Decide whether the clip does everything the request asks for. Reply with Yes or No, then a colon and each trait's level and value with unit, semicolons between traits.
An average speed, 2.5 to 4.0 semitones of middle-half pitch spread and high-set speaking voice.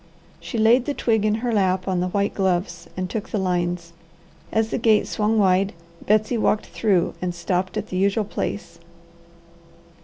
Yes: average, 175 wpm; average, 3.0 semitones; high, 200 Hz